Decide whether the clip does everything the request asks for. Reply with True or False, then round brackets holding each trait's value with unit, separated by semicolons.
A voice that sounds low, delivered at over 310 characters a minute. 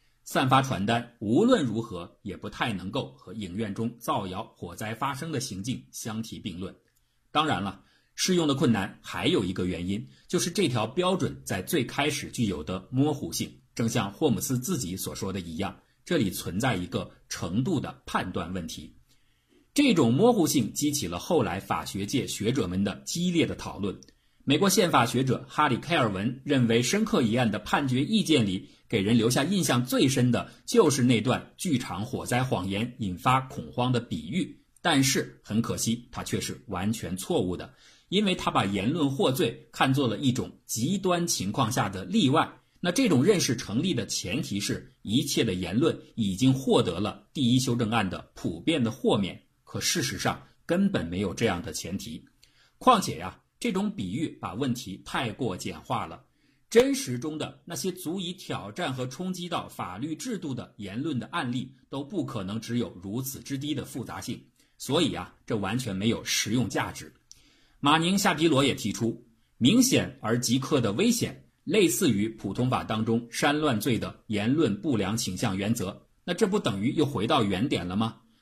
False (125 Hz; 265 characters per minute)